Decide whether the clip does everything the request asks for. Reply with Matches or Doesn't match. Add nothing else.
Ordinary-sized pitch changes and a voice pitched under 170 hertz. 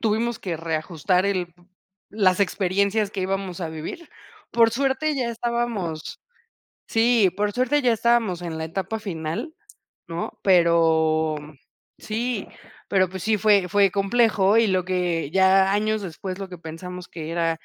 Doesn't match